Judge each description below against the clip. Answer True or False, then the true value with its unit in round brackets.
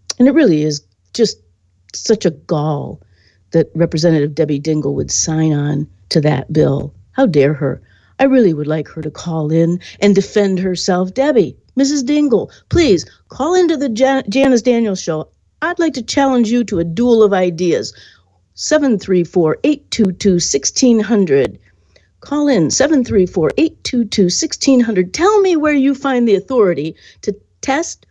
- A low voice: False (190 Hz)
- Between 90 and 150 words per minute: True (140 wpm)